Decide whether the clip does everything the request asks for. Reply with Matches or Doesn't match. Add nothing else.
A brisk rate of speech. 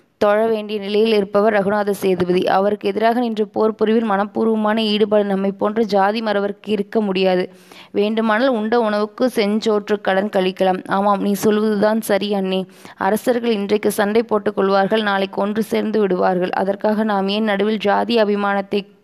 Matches